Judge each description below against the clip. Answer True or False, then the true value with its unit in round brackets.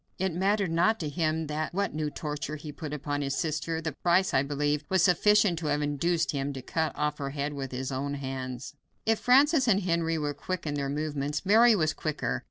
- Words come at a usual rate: False (210 wpm)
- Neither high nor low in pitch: True (155 Hz)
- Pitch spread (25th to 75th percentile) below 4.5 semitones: True (3.5 semitones)